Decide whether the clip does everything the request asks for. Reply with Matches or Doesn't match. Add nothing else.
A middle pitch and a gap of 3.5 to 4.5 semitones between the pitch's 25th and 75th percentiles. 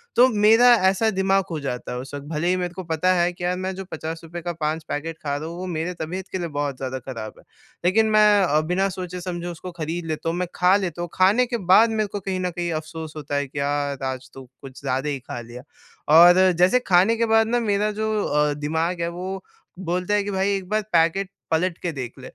Matches